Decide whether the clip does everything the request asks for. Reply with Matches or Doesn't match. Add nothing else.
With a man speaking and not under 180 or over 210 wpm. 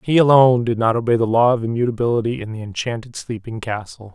Matches